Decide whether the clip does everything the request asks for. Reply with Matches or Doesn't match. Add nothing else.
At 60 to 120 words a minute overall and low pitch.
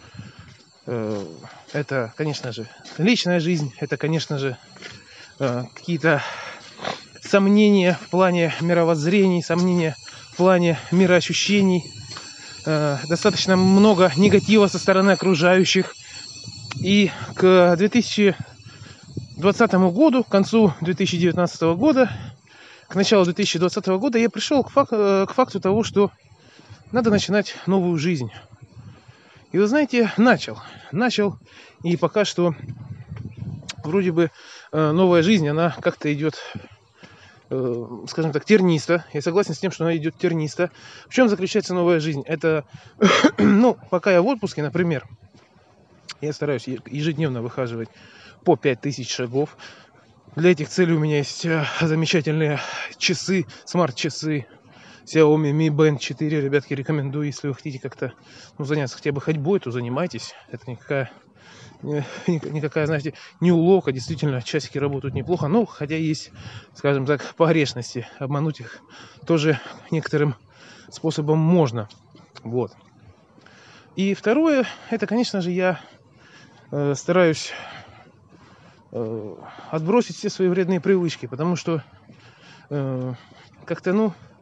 Doesn't match